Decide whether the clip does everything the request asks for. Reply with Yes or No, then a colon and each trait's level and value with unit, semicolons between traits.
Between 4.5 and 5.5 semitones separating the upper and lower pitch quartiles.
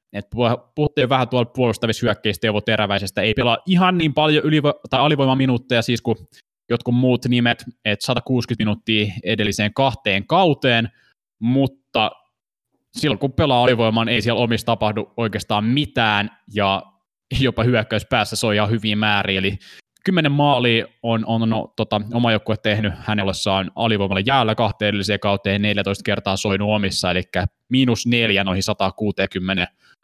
No: average, 3.0 semitones